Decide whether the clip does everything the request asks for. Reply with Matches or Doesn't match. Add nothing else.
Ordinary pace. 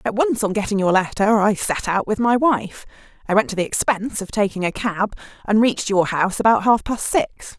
Doesn't match